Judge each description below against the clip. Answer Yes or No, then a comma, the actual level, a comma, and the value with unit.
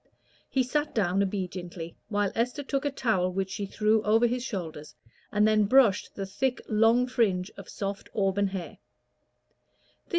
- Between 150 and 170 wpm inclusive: Yes, average, 155 wpm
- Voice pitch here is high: Yes, high, 210 Hz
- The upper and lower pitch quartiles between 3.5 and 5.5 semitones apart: Yes, average, 3.8 semitones